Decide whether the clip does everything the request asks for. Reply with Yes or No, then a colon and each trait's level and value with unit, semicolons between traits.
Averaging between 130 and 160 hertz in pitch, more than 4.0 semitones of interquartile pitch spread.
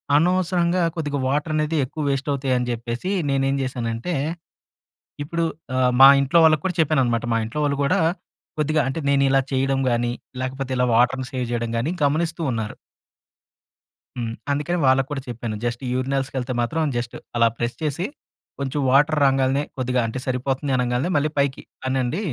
No: low, 135 Hz; average, 3.2 semitones